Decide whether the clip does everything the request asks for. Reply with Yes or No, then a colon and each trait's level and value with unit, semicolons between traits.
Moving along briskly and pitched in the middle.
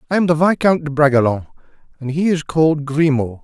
No: average, 190 wpm; medium, 150 Hz